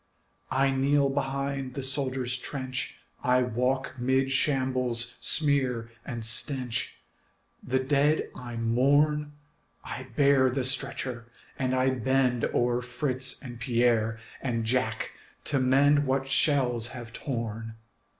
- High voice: No, low, 130 Hz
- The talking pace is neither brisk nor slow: No, slow, 120 wpm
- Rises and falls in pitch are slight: Yes, narrow, 2.0 semitones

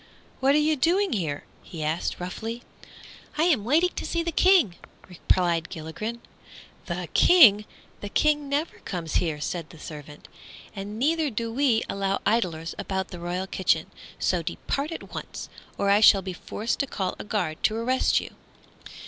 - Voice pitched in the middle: No, high, 210 Hz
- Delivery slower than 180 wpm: Yes, average, 165 wpm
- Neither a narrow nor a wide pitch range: No, wide, 7.9 semitones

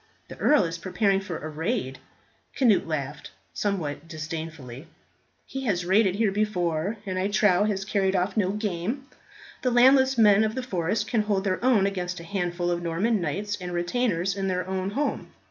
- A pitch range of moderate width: Yes, average, 3.6 semitones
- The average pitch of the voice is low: No, high, 190 Hz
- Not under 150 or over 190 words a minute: Yes, average, 180 wpm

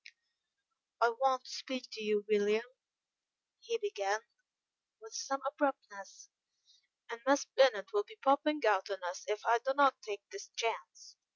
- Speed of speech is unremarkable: Yes, average, 150 wpm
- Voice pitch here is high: Yes, very high, 255 Hz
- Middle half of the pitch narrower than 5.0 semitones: No, wide, 5.4 semitones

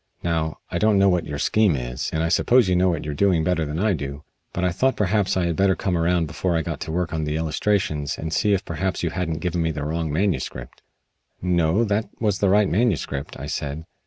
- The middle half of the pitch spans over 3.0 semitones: Yes, average, 3.6 semitones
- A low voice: Yes, very low, 85 Hz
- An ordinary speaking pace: No, fast, 245 wpm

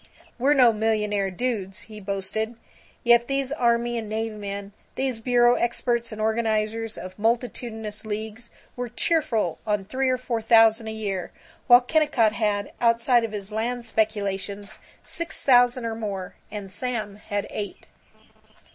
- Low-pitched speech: No, high, 225 Hz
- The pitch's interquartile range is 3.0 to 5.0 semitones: No, narrow, 2.4 semitones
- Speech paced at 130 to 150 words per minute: Yes, average, 145 wpm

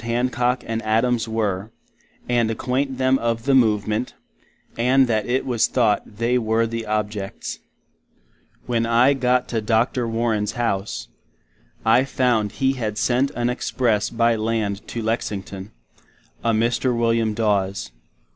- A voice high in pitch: No, low, 115 Hz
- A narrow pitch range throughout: Yes, narrow, 2.3 semitones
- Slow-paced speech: Yes, slow, 130 wpm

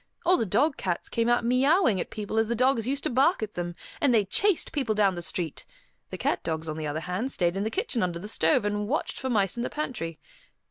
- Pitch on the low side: No, high, 220 Hz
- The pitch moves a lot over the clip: Yes, wide, 6.4 semitones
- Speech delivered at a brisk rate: Yes, fast, 250 wpm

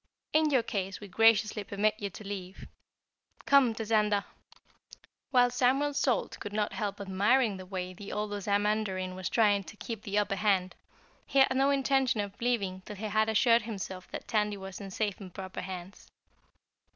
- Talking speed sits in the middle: Yes, average, 175 wpm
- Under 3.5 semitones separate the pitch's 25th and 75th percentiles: Yes, average, 2.8 semitones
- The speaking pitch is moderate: No, high, 210 Hz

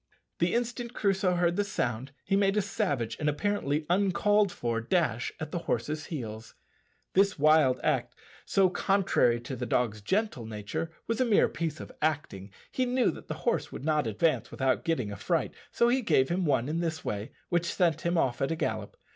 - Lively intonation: Yes, wide, 7.8 semitones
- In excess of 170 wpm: Yes, average, 195 wpm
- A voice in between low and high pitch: Yes, medium, 160 Hz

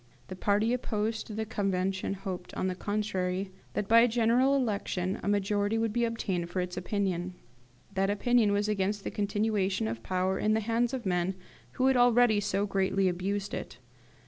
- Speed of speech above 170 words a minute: Yes, average, 180 wpm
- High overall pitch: Yes, high, 205 Hz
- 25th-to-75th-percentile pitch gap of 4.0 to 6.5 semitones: No, average, 2.9 semitones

